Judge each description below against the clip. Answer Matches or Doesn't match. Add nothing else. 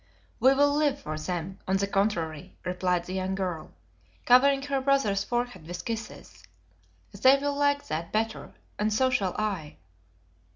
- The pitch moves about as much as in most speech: Doesn't match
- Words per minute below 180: Matches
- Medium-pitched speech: Doesn't match